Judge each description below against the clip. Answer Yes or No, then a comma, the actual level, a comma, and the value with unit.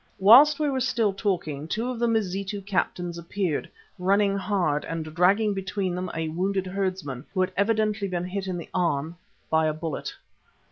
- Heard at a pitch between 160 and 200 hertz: Yes, high, 190 Hz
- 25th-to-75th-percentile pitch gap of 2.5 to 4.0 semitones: Yes, average, 3.1 semitones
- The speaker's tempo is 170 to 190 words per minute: Yes, average, 175 wpm